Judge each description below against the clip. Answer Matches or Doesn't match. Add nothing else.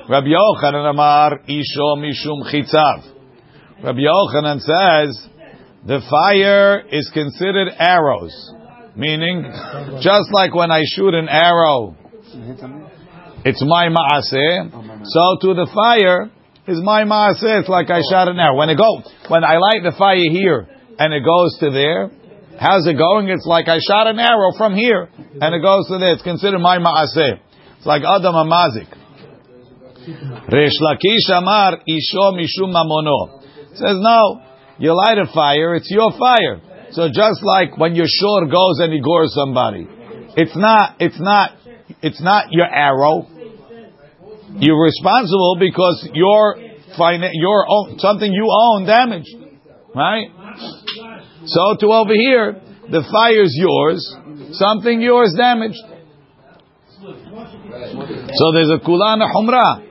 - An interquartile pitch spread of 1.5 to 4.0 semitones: Doesn't match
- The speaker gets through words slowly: Matches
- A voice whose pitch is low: Doesn't match